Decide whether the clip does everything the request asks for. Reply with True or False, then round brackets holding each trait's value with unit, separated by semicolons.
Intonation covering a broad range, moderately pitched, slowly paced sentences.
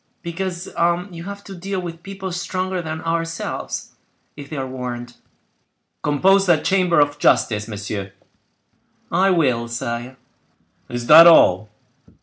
True (6.8 semitones; 165 Hz; 130 wpm)